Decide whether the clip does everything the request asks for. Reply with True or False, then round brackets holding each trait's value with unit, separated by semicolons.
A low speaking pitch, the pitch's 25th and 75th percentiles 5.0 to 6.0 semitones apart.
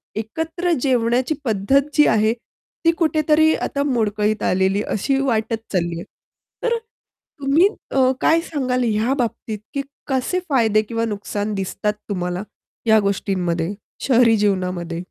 False (225 Hz; 5.3 semitones)